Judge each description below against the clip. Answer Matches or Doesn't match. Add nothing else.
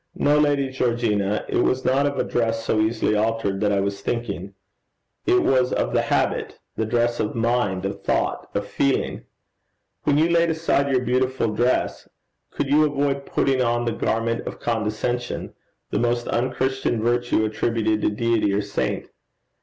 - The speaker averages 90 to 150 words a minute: Doesn't match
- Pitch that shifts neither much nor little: Matches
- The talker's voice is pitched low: Matches